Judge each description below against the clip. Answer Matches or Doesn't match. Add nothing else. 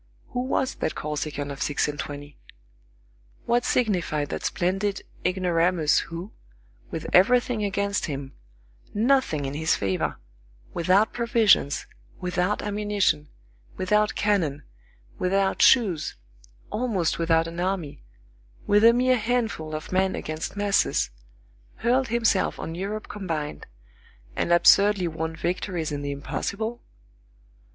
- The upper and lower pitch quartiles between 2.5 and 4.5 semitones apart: Doesn't match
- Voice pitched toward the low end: Doesn't match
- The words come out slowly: Matches